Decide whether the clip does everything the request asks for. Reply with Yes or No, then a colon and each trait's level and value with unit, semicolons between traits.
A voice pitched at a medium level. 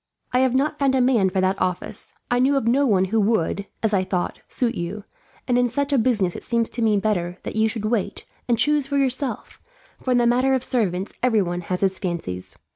No: high, 225 Hz